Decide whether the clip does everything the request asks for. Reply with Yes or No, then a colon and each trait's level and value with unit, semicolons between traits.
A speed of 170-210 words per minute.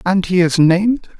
Yes: average, 200 wpm